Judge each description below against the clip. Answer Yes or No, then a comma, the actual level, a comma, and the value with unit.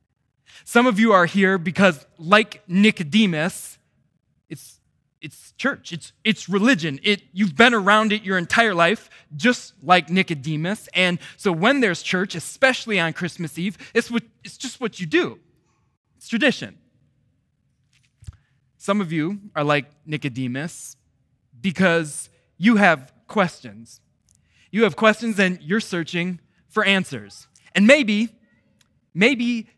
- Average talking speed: No, slow, 130 wpm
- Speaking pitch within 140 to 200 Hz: Yes, medium, 185 Hz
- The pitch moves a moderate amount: No, wide, 6.2 semitones